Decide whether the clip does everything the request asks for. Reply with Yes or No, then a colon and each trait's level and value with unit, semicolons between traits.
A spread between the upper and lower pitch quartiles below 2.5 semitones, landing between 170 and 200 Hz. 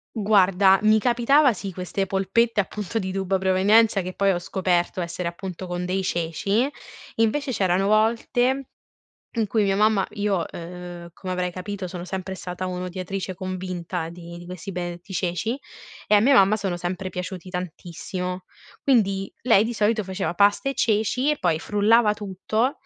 No: average, 2.9 semitones; high, 190 Hz